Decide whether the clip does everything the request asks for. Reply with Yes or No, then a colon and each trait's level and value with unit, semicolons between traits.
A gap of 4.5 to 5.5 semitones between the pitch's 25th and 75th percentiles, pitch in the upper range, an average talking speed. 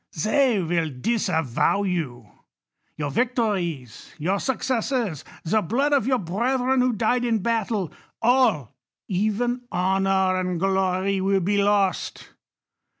No: average, 4.9 semitones; high, 200 Hz; slow, 125 wpm